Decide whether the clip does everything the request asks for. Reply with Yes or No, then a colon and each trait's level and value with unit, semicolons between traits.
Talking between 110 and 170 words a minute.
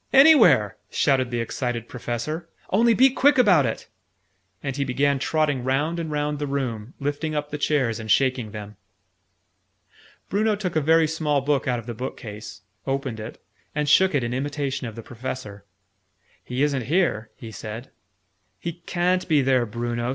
Yes: average, 165 wpm